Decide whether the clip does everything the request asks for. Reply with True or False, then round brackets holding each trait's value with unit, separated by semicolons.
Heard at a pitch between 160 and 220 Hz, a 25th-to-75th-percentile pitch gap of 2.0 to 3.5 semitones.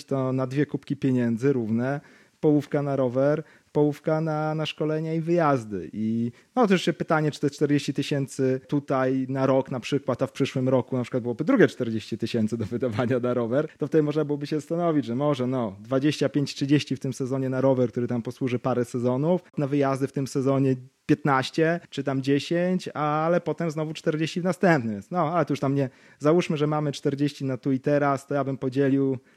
False (140 Hz; 2.7 semitones)